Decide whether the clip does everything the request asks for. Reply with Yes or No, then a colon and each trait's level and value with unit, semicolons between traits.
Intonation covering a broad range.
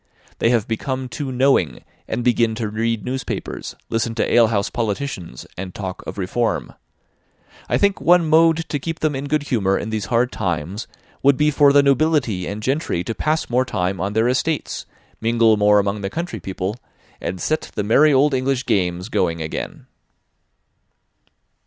Yes: wide, 5.7 semitones